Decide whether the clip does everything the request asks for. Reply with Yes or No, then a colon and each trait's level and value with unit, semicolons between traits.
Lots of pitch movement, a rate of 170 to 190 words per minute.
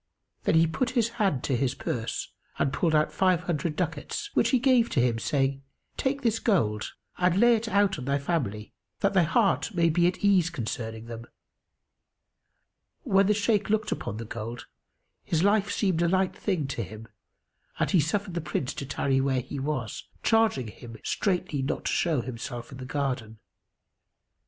Yes: wide, 7.8 semitones; average, 180 wpm